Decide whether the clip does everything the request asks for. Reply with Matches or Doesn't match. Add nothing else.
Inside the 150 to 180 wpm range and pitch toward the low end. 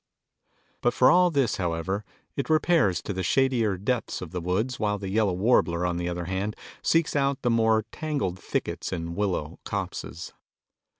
Matches